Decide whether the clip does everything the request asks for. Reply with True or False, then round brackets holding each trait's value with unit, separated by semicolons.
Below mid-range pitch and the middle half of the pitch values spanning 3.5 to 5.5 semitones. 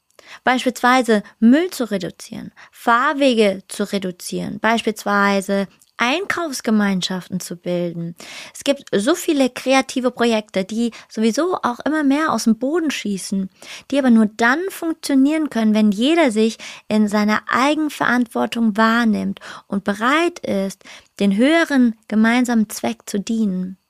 False (225 Hz; 4.7 semitones)